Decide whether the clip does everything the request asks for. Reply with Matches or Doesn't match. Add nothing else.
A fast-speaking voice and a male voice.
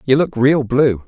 Matches